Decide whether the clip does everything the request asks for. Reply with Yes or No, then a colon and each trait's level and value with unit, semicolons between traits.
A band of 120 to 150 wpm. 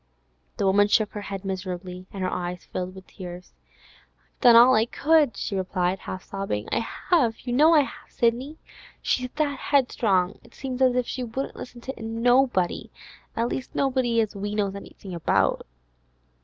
No: average, 170 wpm